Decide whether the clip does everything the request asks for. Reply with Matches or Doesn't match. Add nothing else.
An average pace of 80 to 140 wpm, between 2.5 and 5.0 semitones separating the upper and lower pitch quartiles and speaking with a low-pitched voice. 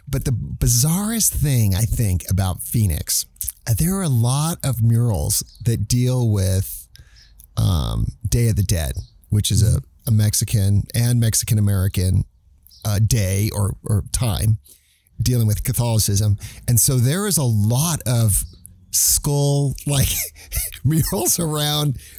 Matches